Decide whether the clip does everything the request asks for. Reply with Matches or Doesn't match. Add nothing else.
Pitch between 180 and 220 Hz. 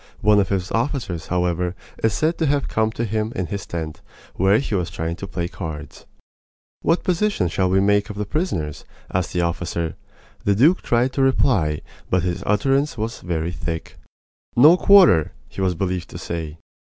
Doesn't match